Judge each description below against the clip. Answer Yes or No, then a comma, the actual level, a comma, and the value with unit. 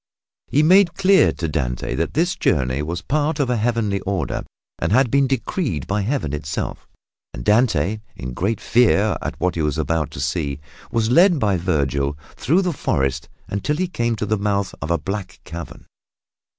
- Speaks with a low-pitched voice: Yes, low, 100 Hz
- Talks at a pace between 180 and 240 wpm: Yes, average, 185 wpm